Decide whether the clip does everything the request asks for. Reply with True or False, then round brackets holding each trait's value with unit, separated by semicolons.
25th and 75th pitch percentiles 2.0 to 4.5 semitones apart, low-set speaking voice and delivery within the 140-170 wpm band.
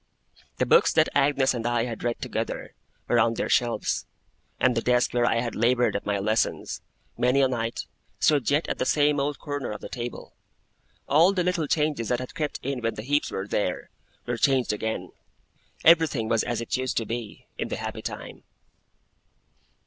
False (3.7 semitones; 125 Hz; 190 wpm)